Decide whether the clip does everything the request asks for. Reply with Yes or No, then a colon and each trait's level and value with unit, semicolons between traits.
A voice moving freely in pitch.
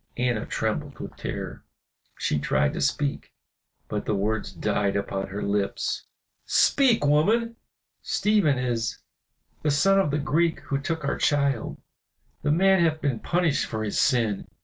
Yes: wide, 7.3 semitones